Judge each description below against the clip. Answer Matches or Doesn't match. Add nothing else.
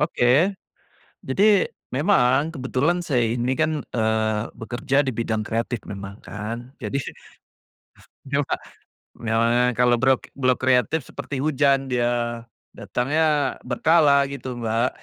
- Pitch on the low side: Matches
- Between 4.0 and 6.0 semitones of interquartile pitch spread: Doesn't match